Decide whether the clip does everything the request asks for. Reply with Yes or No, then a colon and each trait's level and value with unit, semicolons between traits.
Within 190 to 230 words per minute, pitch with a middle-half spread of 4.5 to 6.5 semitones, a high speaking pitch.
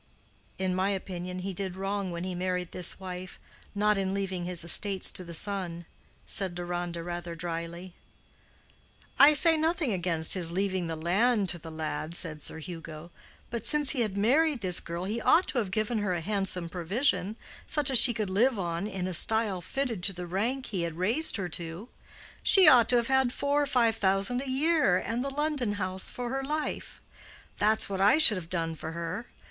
Yes: average, 195 wpm; average, 5.2 semitones; high, 195 Hz